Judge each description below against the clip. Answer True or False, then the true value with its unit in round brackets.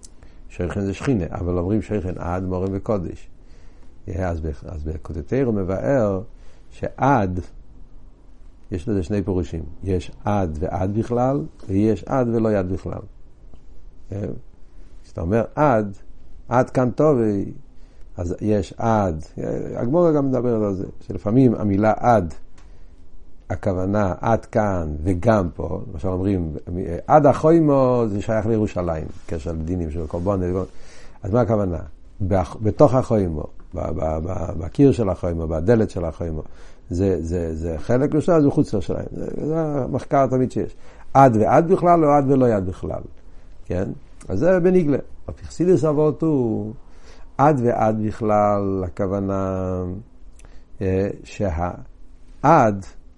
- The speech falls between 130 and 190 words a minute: False (120 wpm)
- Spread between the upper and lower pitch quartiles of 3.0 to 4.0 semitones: False (5.1 semitones)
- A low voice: True (95 Hz)